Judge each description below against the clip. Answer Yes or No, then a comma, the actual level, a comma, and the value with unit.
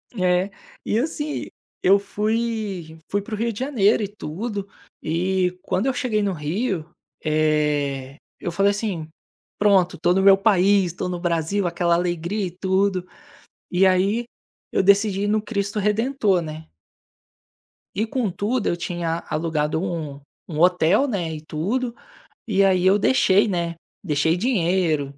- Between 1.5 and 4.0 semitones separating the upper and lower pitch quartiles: Yes, average, 3.6 semitones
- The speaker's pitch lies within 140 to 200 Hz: Yes, high, 190 Hz